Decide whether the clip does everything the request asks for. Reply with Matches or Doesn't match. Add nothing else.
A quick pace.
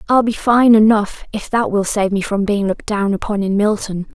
Matches